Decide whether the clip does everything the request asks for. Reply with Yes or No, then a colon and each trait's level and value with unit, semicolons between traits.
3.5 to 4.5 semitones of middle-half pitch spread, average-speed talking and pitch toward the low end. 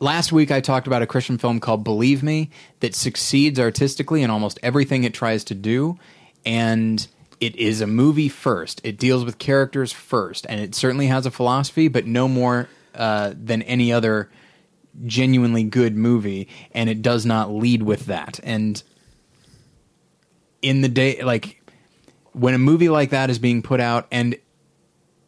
No: average, 2.9 semitones; average, 165 wpm; low, 125 Hz